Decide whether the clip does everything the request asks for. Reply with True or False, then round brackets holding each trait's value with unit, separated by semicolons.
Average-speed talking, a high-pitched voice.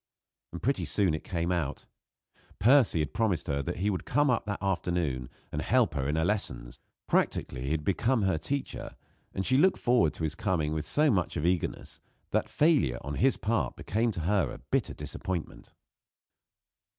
False (185 wpm; 90 Hz)